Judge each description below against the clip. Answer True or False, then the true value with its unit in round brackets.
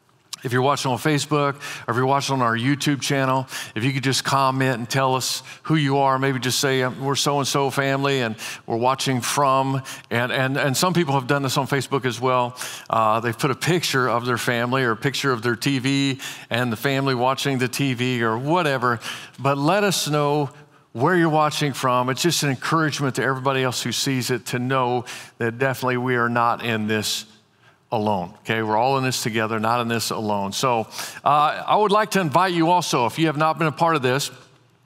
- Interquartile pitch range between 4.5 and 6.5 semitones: False (2.4 semitones)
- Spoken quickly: True (215 wpm)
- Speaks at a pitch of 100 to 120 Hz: False (135 Hz)